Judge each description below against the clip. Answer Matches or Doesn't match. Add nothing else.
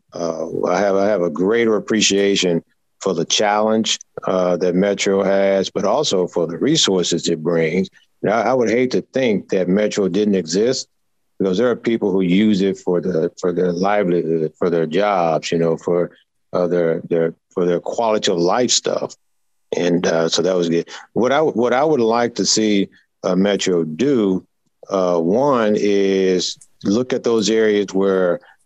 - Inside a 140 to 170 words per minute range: Doesn't match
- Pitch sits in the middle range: Doesn't match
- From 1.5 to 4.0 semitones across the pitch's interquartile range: Matches